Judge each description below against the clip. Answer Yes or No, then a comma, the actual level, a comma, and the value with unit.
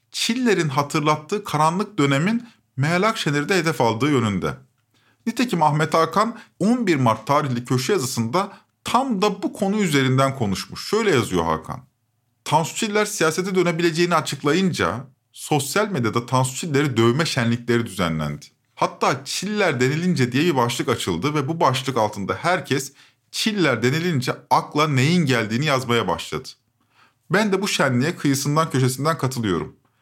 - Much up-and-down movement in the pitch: Yes, wide, 6.3 semitones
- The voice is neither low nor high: Yes, medium, 145 Hz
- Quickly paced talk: No, average, 130 wpm